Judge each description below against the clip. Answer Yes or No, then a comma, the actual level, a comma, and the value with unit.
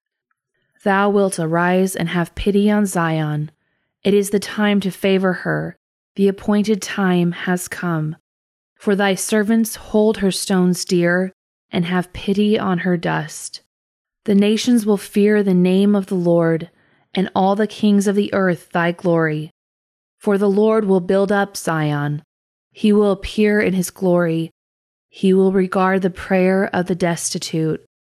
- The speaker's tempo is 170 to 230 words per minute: No, average, 155 wpm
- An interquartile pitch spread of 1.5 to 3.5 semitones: Yes, average, 3.0 semitones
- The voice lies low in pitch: No, high, 190 Hz